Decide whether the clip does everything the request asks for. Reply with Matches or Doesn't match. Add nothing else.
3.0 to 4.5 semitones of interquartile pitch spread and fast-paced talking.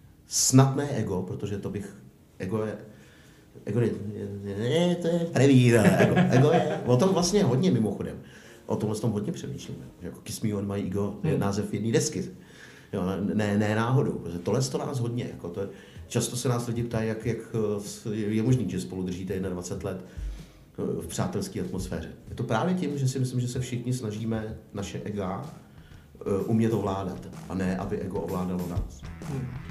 Matches